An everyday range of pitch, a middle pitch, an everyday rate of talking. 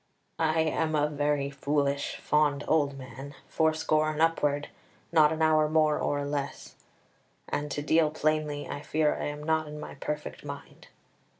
No: narrow, 1.5 semitones; medium, 150 Hz; average, 160 wpm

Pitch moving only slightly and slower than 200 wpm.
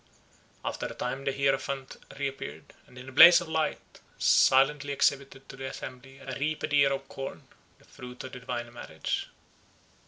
Yes: narrow, 1.3 semitones; average, 165 wpm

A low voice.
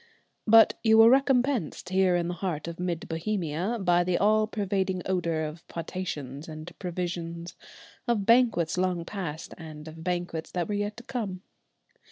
No: medium, 180 Hz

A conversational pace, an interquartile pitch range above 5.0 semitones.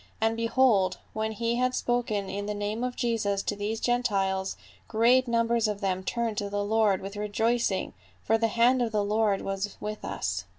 No: average, 185 wpm; narrow, 2.5 semitones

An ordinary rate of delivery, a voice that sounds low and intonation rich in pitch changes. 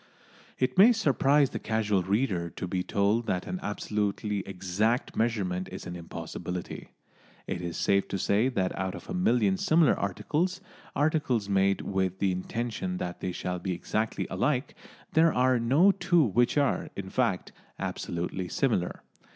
Yes: average, 155 wpm; low, 105 Hz; wide, 6.3 semitones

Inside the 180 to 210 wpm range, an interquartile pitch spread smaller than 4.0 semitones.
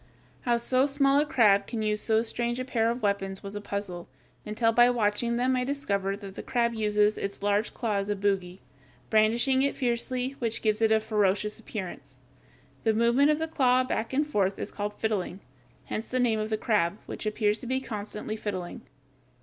Yes: average, 200 wpm; average, 3.1 semitones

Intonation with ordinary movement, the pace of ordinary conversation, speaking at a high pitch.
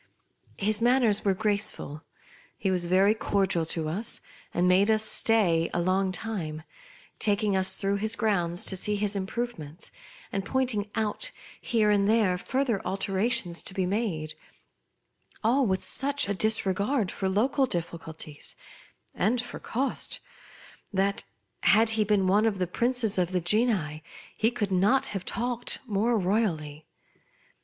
Yes: average, 3.4 semitones; average, 150 wpm; high, 200 Hz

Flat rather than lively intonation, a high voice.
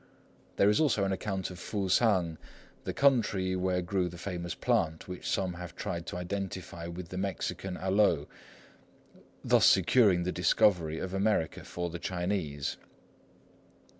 No: narrow, 2.2 semitones; very low, 90 Hz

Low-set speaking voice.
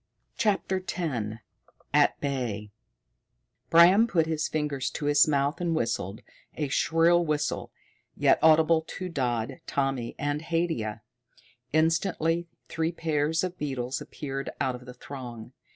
No: medium, 150 Hz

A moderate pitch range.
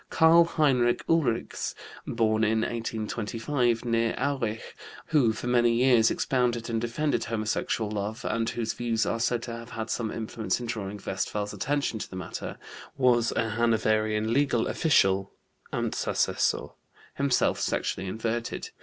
No: narrow, 1.9 semitones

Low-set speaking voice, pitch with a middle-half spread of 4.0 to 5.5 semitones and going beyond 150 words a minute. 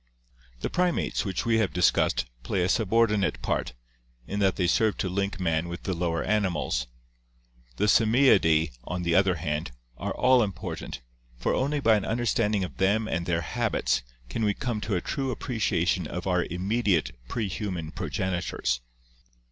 Yes: very low, 95 Hz; average, 4.3 semitones; average, 170 wpm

